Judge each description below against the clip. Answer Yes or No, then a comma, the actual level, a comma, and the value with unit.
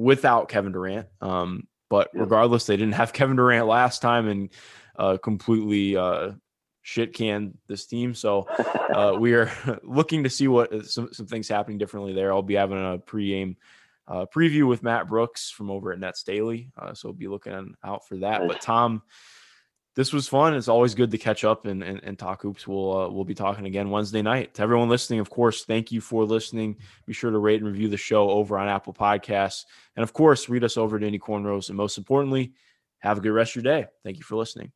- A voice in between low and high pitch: No, low, 110 Hz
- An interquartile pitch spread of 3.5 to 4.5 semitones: No, average, 2.9 semitones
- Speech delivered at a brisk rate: Yes, fast, 215 wpm